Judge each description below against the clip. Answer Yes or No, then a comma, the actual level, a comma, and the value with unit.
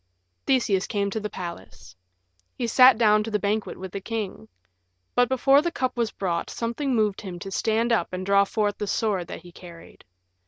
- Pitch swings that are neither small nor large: Yes, average, 3.6 semitones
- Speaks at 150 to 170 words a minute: No, average, 195 wpm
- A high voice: Yes, high, 210 Hz